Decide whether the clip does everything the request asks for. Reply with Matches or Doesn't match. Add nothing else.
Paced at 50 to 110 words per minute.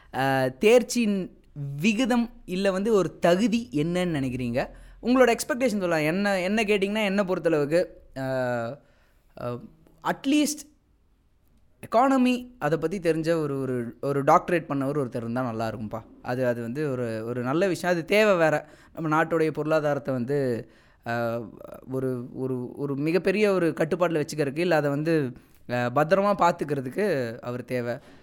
Doesn't match